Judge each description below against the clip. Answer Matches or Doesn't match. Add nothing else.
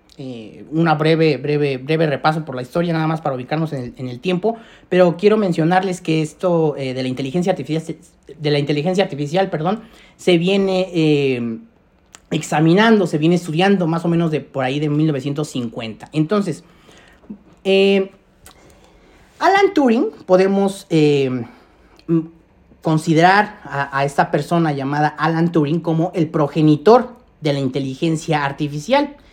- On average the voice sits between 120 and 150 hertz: Doesn't match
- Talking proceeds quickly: Doesn't match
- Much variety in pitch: Doesn't match